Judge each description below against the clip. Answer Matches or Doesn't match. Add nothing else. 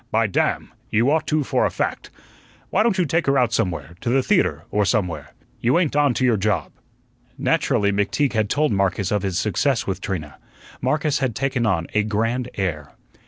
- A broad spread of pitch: Matches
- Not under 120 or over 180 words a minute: Doesn't match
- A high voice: Doesn't match